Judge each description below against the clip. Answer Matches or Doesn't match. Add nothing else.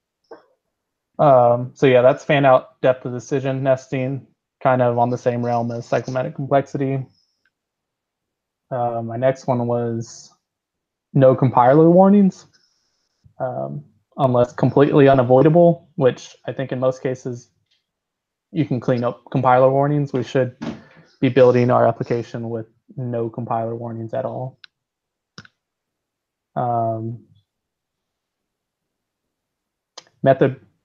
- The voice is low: Matches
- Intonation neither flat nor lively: Doesn't match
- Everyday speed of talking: Doesn't match